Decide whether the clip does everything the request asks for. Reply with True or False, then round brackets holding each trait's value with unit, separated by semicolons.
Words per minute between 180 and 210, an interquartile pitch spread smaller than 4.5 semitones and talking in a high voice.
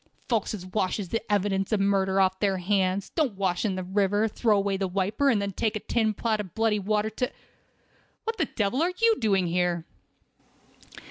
True (195 wpm; 2.4 semitones; 200 Hz)